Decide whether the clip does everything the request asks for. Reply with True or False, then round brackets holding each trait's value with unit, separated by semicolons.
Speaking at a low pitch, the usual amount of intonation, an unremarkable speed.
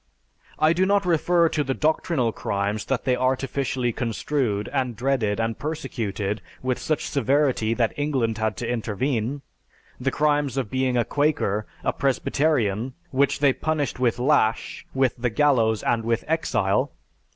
True (130 Hz; 4.4 semitones; 150 wpm)